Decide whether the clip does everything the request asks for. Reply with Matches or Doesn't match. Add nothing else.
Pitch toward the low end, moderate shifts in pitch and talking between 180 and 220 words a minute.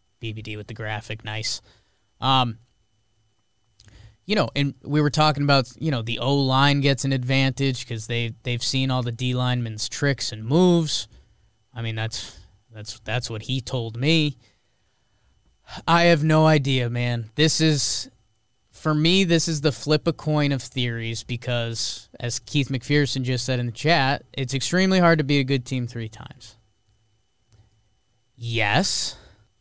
Doesn't match